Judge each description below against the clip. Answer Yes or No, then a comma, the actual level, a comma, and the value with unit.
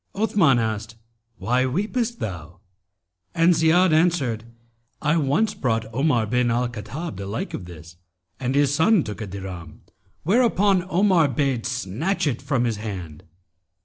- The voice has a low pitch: Yes, low, 130 Hz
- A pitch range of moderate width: No, wide, 7.4 semitones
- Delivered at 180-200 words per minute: No, average, 145 wpm